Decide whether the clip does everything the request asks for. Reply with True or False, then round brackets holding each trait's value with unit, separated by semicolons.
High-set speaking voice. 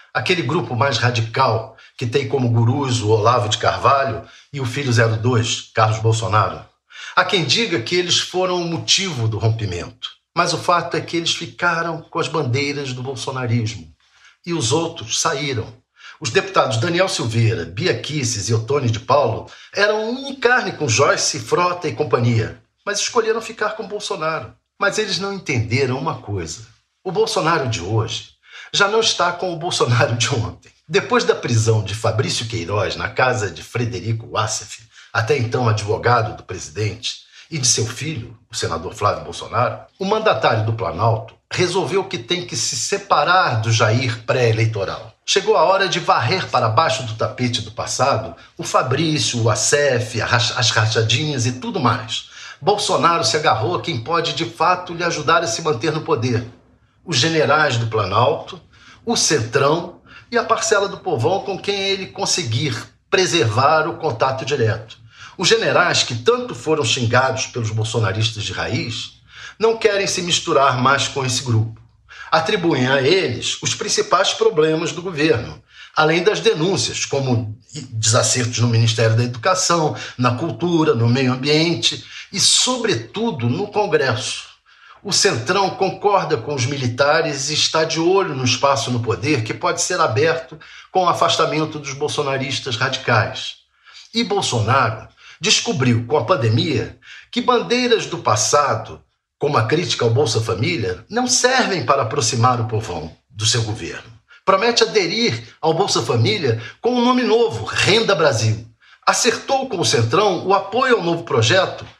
False (135 Hz)